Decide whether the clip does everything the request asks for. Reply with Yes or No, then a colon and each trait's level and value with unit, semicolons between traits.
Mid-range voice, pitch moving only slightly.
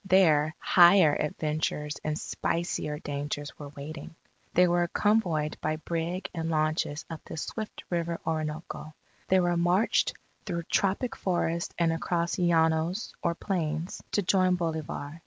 Yes: medium, 165 Hz; narrow, 2.3 semitones